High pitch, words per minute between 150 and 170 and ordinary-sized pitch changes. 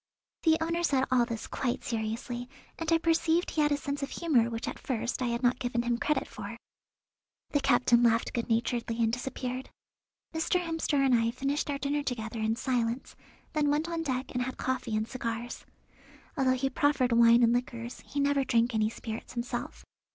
No: very high, 250 Hz; average, 190 wpm; average, 3.4 semitones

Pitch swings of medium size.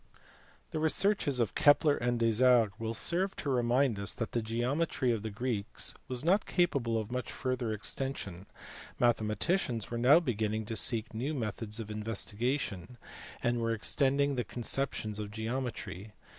Yes: average, 3.5 semitones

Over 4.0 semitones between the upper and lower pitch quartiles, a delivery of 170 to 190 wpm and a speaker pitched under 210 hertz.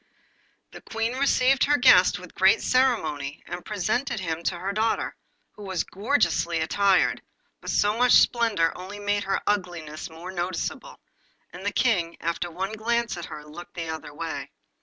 No: average, 5.0 semitones; average, 160 wpm; high, 190 Hz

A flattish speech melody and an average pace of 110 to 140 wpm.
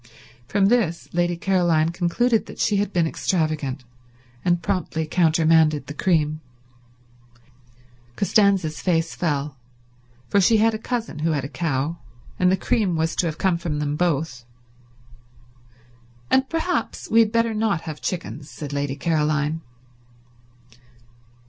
No: average, 4.2 semitones; slow, 135 wpm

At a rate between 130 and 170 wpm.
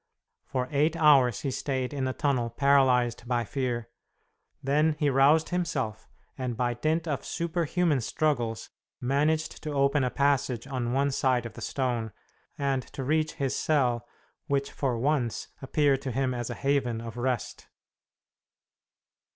Yes: average, 150 wpm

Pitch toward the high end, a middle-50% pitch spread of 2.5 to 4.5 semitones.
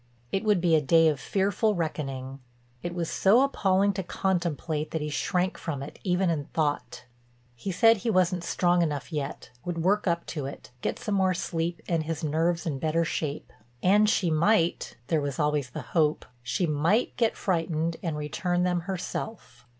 No: medium, 170 Hz; average, 3.7 semitones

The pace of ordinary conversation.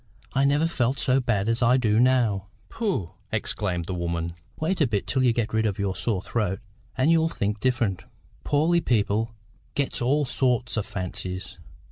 Yes: average, 175 wpm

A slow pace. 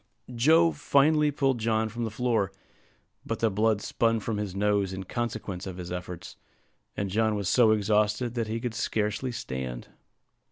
No: average, 165 wpm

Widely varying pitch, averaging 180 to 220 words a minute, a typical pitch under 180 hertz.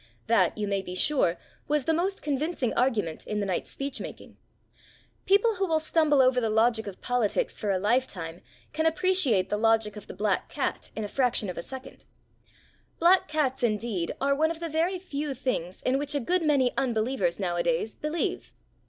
No: wide, 6.5 semitones; average, 190 wpm; very high, 255 Hz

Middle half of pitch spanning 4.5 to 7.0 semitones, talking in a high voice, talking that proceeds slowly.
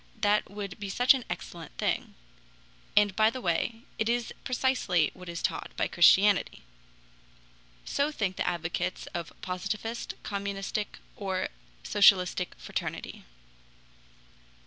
No: average, 3.4 semitones; high, 200 Hz; slow, 120 wpm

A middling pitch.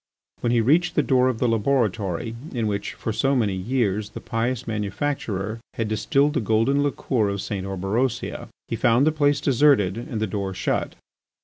No: low, 115 Hz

